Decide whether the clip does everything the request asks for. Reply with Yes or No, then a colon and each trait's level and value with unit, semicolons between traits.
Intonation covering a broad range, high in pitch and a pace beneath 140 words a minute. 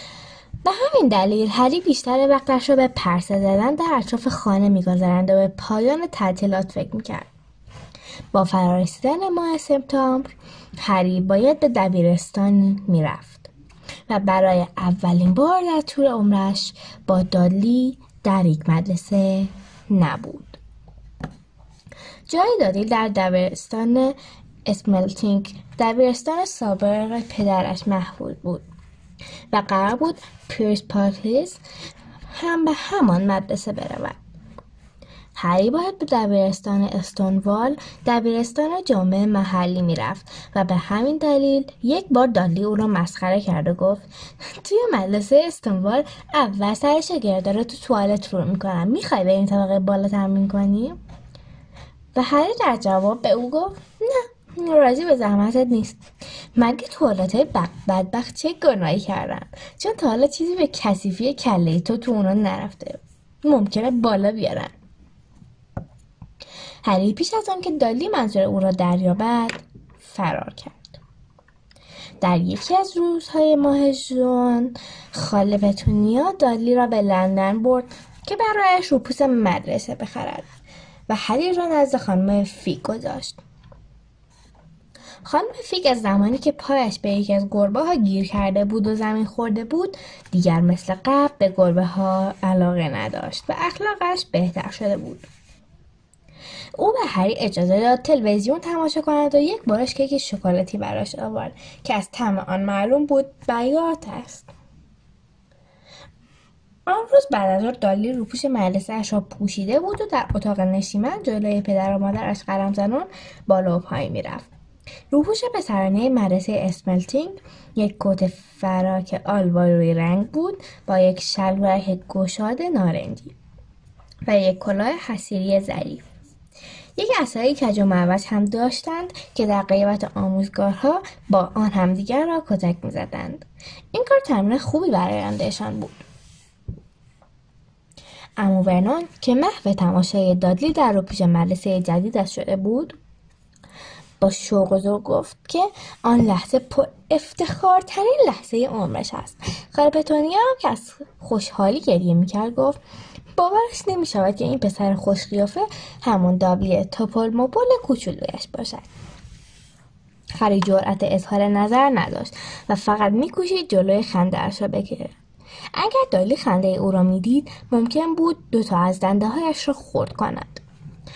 Yes: wide, 6.2 semitones; high, 205 Hz; average, 130 wpm